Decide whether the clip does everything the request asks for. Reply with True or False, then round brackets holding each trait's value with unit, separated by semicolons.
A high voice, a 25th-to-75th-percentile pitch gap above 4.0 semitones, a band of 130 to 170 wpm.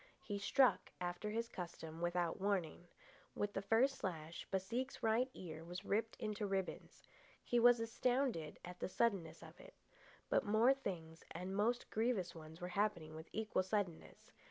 True (195 Hz; 4.6 semitones; 155 wpm)